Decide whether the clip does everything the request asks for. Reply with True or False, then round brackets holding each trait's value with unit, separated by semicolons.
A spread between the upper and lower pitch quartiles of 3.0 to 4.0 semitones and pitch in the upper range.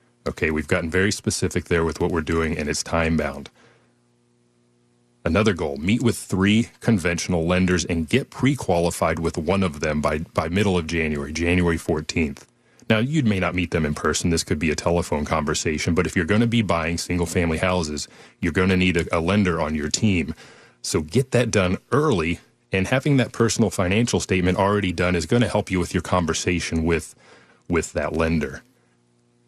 False (3.4 semitones; 85 Hz)